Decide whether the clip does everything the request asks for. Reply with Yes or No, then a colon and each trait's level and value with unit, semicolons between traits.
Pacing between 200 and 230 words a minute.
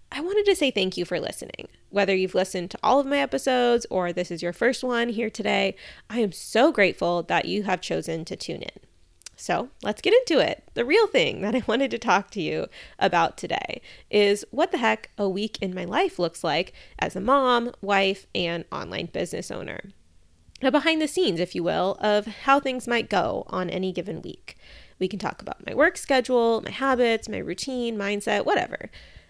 Yes: fast, 205 wpm